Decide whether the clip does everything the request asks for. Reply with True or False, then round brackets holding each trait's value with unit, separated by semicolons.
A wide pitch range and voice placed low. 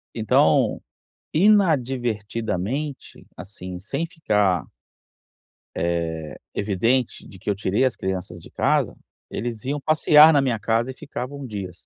True (6.1 semitones; 115 Hz)